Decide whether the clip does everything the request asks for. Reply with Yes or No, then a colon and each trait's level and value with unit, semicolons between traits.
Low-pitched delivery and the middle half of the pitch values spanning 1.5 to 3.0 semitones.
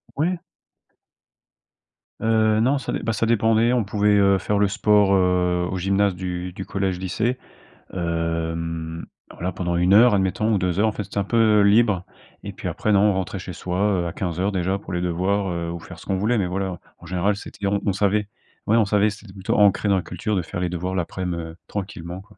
Yes: very low, 95 Hz; average, 2.7 semitones